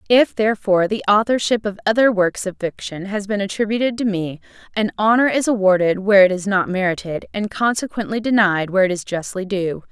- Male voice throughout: No, female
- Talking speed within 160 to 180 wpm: No, average, 190 wpm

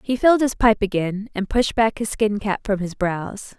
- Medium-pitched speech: No, high, 210 Hz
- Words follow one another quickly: Yes, fast, 235 wpm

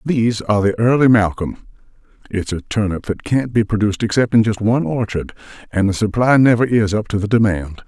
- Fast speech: No, average, 190 wpm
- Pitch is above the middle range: No, low, 110 Hz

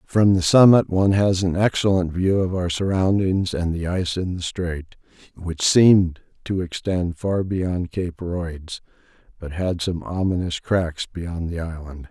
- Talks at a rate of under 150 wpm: No, average, 165 wpm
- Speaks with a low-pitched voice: Yes, very low, 90 Hz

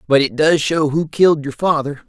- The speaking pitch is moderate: Yes, medium, 150 Hz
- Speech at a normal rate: No, fast, 230 wpm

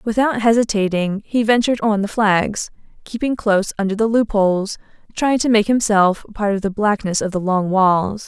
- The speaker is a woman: Yes, female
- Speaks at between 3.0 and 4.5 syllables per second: No, 5.1 syllables/s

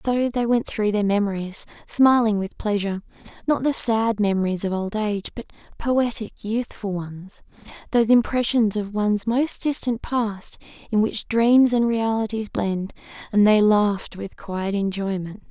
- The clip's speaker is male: No, female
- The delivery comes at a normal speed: Yes, average, 145 wpm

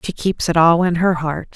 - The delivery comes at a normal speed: No, fast, 270 wpm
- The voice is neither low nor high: Yes, medium, 170 Hz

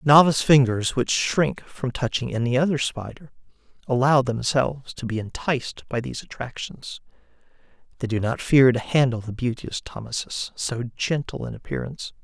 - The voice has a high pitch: No, low, 130 Hz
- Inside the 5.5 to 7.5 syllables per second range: No, 5.1 syllables/s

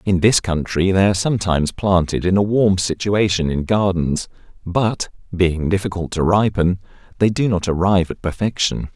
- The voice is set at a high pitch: No, very low, 95 Hz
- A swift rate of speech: No, average, 160 wpm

